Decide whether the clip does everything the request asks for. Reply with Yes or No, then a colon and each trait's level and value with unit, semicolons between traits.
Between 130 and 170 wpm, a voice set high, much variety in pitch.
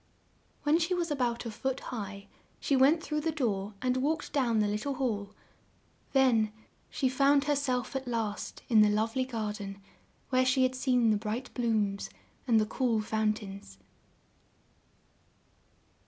No: average, 160 wpm; high, 245 Hz; average, 4.0 semitones